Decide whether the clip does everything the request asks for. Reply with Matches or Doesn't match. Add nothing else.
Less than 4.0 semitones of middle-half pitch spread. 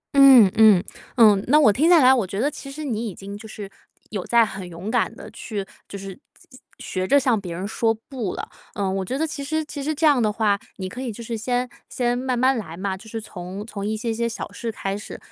Doesn't match